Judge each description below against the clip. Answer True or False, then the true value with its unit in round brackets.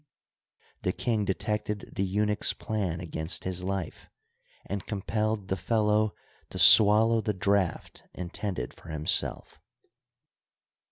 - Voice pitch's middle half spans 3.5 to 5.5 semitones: False (2.5 semitones)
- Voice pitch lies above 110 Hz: False (100 Hz)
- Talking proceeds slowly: True (110 wpm)